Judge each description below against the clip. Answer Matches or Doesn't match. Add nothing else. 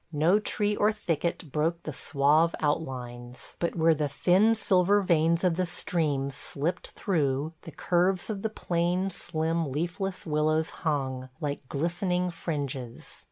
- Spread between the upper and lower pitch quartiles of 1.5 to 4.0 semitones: Matches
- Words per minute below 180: Matches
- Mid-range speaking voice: Matches